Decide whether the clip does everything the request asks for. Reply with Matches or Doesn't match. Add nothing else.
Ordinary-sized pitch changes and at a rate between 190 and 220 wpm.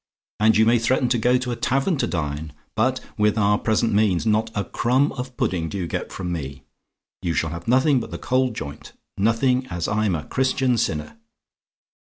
Doesn't match